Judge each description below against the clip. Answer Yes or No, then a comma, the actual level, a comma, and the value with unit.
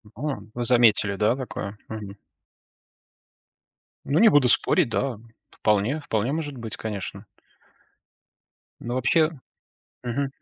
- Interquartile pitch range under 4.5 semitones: No, average, 4.8 semitones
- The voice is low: Yes, low, 120 Hz